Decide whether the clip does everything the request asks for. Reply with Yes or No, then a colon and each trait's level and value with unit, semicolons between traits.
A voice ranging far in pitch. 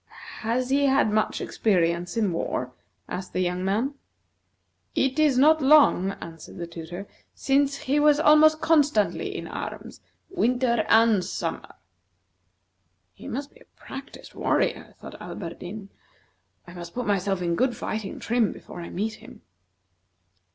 Yes: wide, 7.3 semitones